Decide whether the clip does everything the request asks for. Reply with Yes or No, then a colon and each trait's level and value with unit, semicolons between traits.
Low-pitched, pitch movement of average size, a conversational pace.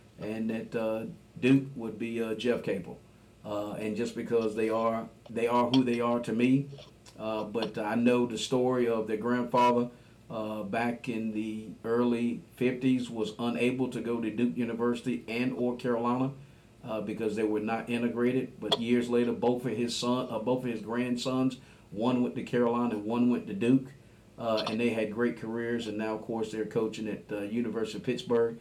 No: low, 120 Hz; narrow, 1.7 semitones; average, 190 wpm